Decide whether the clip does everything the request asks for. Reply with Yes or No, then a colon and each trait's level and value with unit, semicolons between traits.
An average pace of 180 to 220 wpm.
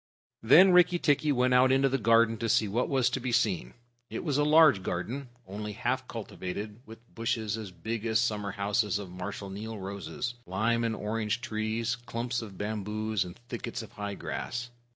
Yes: average, 185 wpm